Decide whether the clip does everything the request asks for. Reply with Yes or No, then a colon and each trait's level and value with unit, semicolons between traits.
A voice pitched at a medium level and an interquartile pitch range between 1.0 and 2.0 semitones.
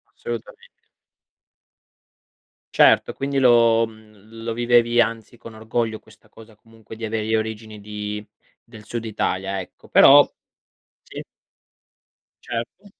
No: low, 115 Hz; narrow, 1.6 semitones